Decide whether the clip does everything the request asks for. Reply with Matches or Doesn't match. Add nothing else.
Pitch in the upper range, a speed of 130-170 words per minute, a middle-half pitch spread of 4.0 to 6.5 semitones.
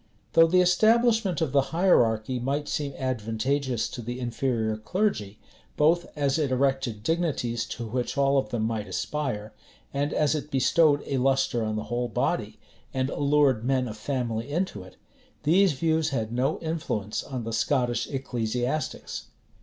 Doesn't match